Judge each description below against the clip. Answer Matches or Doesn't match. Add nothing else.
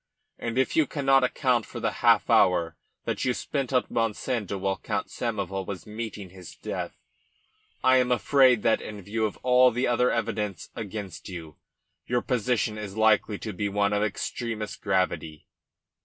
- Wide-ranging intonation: Doesn't match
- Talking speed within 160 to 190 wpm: Matches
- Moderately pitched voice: Doesn't match